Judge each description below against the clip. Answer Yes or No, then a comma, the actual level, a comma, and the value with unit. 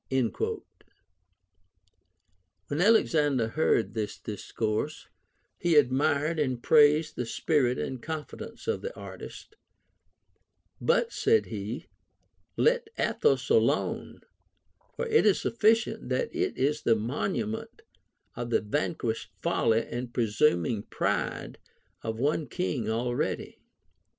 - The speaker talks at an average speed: No, slow, 110 wpm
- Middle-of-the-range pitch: Yes, medium, 145 Hz